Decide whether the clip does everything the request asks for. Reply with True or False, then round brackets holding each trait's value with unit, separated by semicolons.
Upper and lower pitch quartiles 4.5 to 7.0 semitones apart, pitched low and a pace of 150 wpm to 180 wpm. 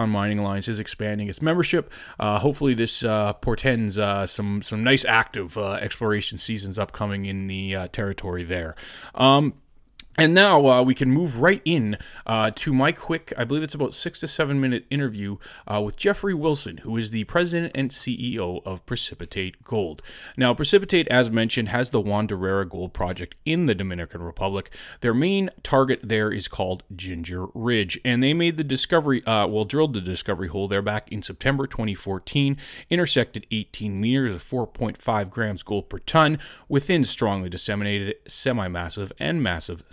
True (5.4 semitones; 110 Hz; 170 wpm)